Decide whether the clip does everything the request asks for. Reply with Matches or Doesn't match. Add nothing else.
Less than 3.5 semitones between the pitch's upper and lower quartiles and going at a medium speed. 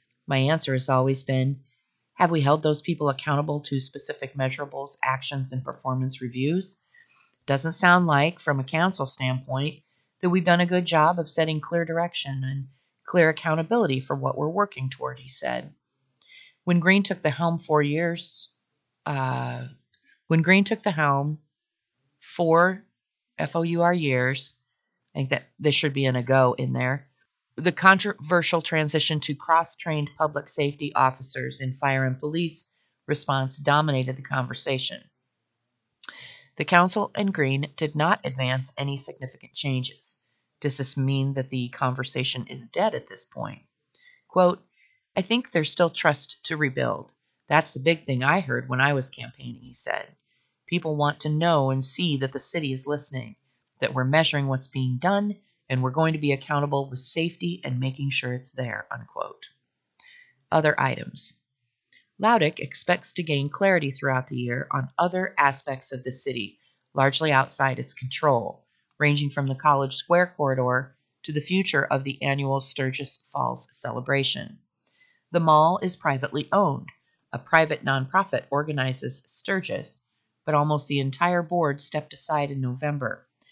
Doesn't match